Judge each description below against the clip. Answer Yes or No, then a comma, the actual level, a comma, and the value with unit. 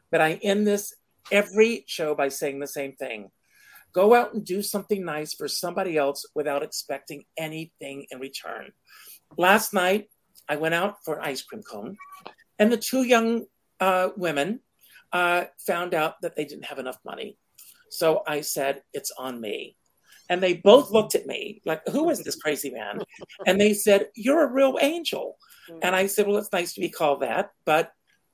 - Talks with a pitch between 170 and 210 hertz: Yes, medium, 185 Hz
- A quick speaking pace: No, average, 180 wpm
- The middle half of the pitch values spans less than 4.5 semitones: No, average, 5.3 semitones